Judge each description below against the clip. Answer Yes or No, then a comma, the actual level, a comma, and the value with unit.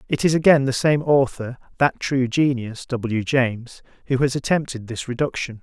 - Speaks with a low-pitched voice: Yes, low, 130 Hz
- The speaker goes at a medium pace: Yes, average, 170 wpm